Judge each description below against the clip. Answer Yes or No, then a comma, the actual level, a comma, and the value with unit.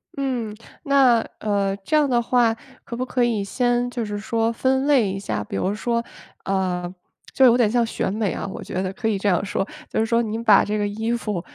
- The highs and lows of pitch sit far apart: No, average, 3.3 semitones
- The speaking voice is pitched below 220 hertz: No, high, 225 Hz